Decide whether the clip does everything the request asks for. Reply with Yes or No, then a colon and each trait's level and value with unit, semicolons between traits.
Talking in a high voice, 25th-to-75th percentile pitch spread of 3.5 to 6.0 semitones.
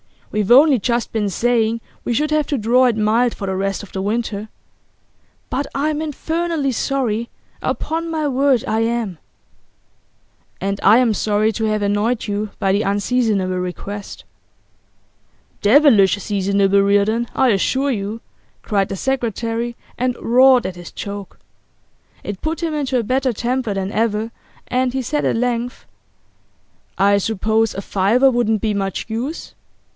Yes: high, 225 Hz; average, 4.1 semitones